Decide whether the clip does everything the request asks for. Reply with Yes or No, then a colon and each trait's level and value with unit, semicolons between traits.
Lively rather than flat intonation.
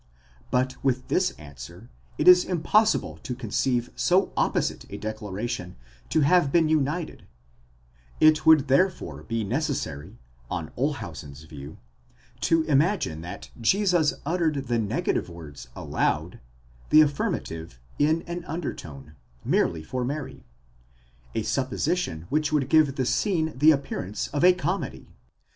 Yes: wide, 8.3 semitones